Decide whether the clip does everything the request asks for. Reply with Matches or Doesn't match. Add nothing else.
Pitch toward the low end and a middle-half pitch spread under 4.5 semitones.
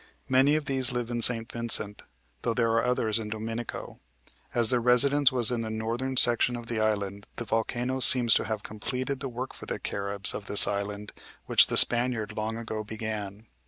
Matches